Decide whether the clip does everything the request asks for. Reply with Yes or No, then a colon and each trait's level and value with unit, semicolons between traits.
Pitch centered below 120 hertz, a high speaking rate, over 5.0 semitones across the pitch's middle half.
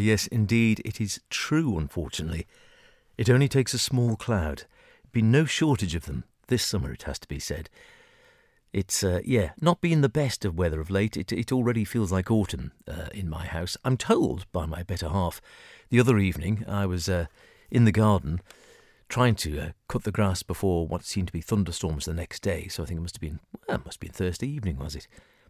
Yes: low, 100 Hz; fast, 215 wpm; wide, 5.6 semitones